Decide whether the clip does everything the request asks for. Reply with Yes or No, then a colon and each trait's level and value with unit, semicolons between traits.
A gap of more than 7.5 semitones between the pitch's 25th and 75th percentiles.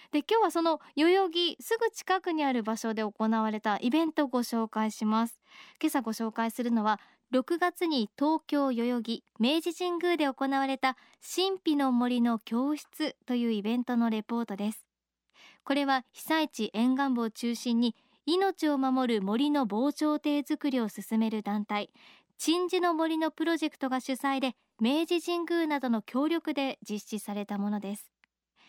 No: wide, 5.6 semitones